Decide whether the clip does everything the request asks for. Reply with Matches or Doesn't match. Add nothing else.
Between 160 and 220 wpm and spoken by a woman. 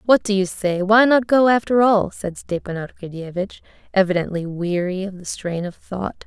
Matches